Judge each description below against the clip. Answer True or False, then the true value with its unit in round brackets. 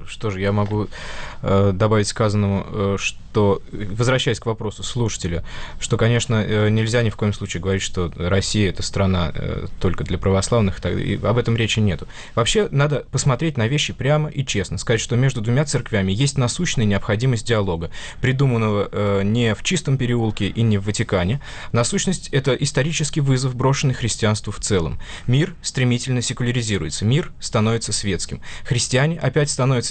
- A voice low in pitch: True (110 Hz)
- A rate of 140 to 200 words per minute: True (160 wpm)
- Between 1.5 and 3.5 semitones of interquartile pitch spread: False (4.5 semitones)